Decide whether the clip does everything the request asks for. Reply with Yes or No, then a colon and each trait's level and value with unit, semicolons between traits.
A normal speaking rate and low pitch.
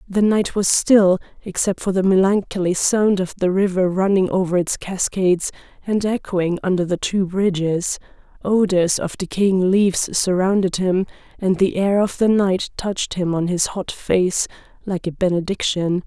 No: average, 160 wpm; high, 190 Hz